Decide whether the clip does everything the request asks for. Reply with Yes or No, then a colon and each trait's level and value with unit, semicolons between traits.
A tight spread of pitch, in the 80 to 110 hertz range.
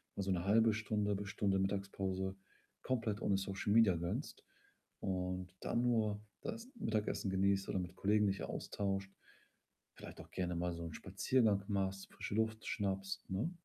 Yes: narrow, 2.0 semitones; low, 100 Hz